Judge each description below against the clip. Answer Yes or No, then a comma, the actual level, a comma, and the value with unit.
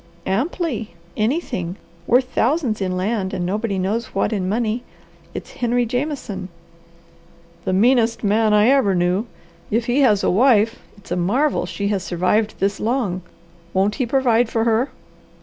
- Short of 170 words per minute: Yes, average, 150 wpm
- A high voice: Yes, high, 220 Hz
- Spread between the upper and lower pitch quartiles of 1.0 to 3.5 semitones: No, average, 4.1 semitones